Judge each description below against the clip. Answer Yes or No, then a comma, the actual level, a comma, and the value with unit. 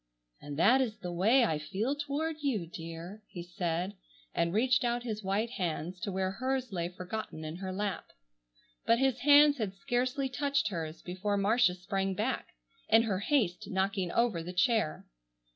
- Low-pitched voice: No, high, 200 Hz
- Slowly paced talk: No, average, 170 wpm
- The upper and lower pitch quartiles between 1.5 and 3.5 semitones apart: No, wide, 5.4 semitones